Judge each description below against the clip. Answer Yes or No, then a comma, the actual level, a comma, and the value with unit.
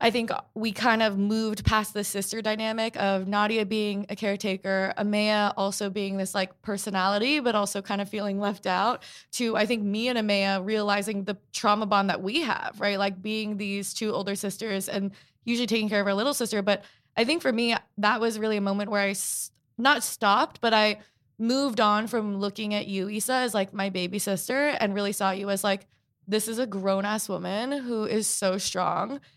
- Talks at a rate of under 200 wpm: No, fast, 205 wpm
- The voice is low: No, high, 205 Hz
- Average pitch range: No, narrow, 1.8 semitones